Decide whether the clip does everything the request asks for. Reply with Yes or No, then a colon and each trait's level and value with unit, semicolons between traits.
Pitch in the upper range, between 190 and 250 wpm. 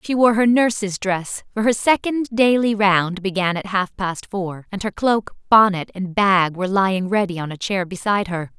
Yes: high, 200 Hz; fast, 205 wpm